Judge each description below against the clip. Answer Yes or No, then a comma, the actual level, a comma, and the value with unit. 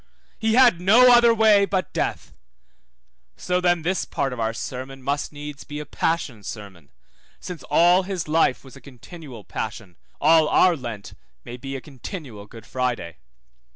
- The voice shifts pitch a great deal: Yes, wide, 6.7 semitones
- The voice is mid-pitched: Yes, medium, 145 Hz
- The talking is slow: No, average, 165 wpm